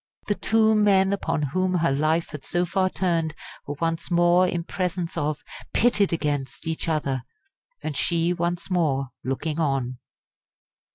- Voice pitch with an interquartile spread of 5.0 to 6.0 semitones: No, average, 3.5 semitones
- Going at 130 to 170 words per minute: Yes, average, 150 wpm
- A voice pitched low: No, medium, 165 Hz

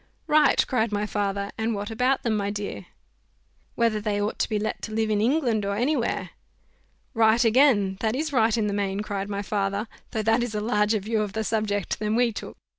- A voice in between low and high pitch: No, high, 215 Hz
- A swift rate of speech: Yes, fast, 215 wpm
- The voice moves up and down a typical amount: No, narrow, 2.1 semitones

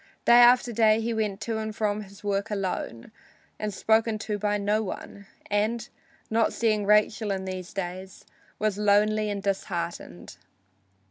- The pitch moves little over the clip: Yes, narrow, 1.8 semitones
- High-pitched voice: Yes, high, 210 Hz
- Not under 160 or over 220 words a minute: No, average, 145 wpm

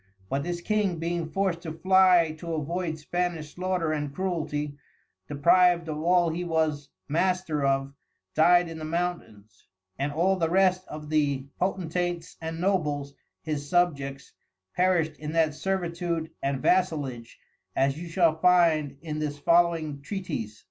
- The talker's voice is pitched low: No, medium, 165 Hz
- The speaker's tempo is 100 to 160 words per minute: Yes, average, 145 wpm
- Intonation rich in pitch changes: No, average, 3.1 semitones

